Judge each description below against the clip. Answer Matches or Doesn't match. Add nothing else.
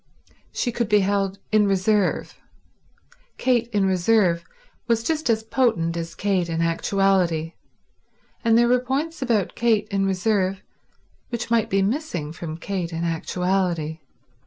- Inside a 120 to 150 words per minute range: Matches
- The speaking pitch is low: Doesn't match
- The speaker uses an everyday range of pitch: Matches